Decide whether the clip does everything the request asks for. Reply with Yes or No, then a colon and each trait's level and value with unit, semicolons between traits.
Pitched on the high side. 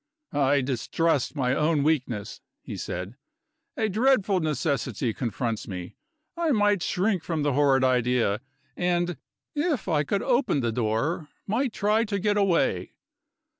No: medium, 155 Hz